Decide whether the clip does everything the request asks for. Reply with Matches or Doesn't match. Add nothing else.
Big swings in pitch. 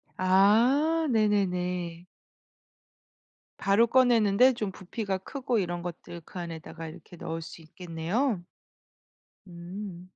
Doesn't match